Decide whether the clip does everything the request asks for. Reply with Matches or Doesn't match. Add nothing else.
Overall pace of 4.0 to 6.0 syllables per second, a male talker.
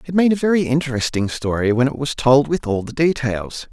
Matches